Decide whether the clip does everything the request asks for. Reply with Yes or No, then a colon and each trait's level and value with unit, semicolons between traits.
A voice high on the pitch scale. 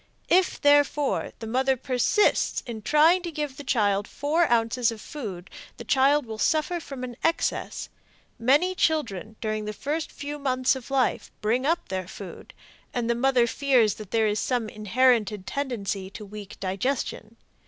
Yes: very high, 250 Hz